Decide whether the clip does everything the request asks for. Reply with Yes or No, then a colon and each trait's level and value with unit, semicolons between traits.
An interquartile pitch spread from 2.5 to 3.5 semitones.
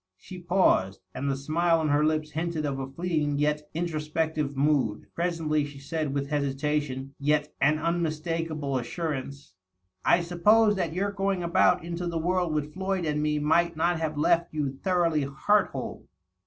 Yes: average, 2.9 semitones